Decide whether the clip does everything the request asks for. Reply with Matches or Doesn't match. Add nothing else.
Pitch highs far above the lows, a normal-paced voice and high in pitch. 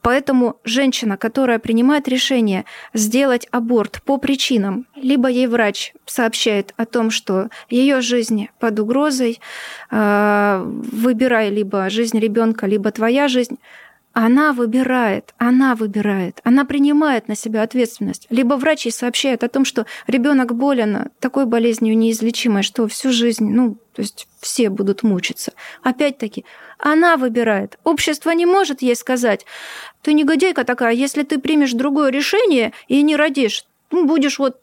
Doesn't match